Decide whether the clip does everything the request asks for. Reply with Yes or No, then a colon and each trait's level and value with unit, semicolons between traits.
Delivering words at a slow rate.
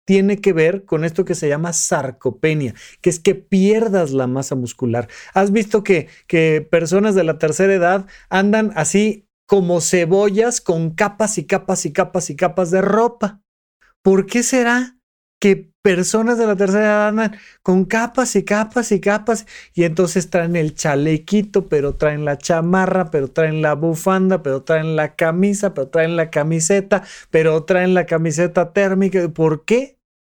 No: average, 165 wpm